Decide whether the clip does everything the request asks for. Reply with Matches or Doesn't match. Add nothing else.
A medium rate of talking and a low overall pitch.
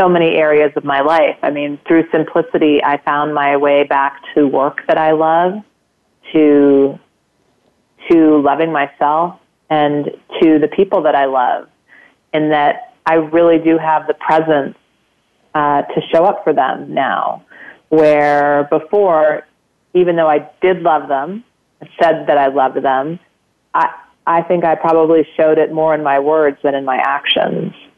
Doesn't match